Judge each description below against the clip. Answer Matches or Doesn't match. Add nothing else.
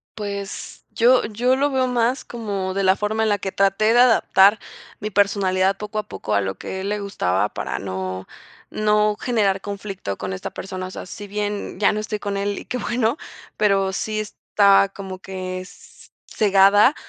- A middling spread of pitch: Doesn't match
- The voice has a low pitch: Doesn't match